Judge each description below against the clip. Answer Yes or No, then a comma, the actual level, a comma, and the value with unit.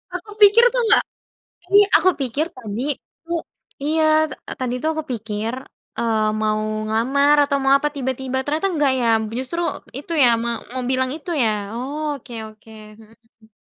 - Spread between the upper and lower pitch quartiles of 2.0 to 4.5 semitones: No, average, 5.0 semitones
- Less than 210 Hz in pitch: No, very high, 260 Hz